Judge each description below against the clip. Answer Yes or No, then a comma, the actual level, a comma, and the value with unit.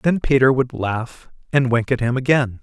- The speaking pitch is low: Yes, low, 125 Hz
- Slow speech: No, fast, 205 wpm